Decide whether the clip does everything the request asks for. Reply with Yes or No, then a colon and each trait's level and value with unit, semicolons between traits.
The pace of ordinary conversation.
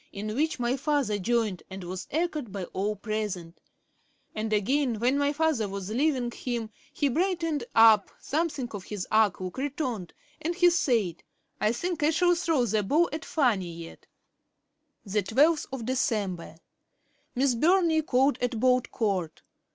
Yes: average, 150 wpm